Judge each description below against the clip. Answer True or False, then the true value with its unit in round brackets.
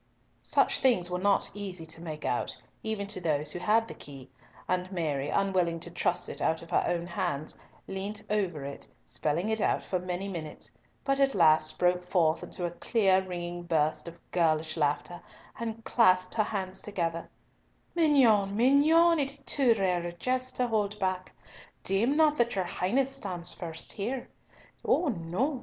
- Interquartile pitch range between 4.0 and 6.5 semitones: True (4.7 semitones)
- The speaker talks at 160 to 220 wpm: True (175 wpm)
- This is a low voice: False (185 Hz)